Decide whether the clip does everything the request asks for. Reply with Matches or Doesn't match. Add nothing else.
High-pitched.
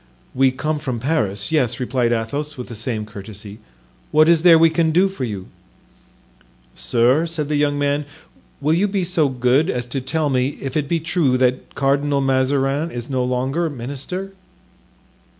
Doesn't match